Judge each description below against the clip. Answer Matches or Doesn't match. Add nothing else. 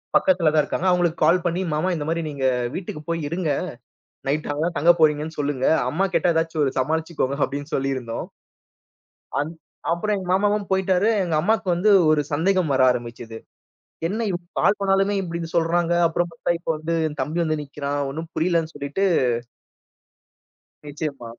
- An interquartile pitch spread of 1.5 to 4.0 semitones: Matches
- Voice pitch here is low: Doesn't match